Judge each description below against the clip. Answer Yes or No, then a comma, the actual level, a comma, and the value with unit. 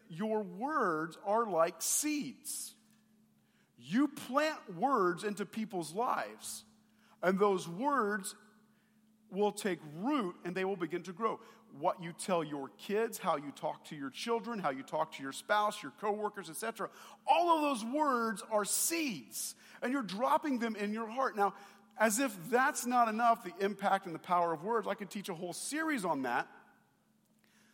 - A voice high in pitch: Yes, high, 210 Hz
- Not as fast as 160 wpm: No, average, 165 wpm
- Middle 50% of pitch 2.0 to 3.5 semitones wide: No, average, 4.1 semitones